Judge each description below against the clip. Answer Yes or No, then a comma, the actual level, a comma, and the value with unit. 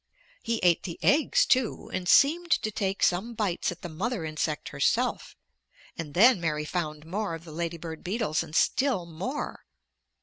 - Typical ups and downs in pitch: No, wide, 5.9 semitones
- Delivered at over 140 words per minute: Yes, average, 170 wpm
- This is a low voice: No, medium, 180 Hz